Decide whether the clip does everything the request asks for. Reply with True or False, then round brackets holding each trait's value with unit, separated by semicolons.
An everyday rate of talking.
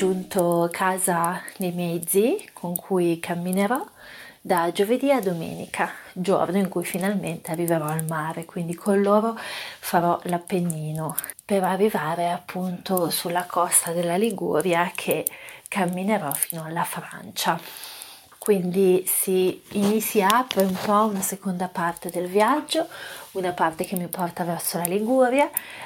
True (125 wpm)